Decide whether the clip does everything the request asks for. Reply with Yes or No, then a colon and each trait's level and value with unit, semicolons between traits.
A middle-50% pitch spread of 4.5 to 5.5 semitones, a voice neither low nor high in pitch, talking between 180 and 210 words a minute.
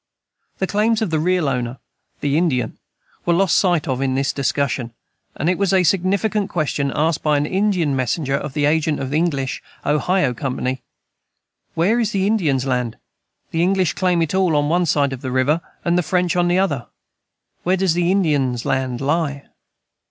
Yes: average, 4.9 semitones; medium, 155 Hz; average, 185 wpm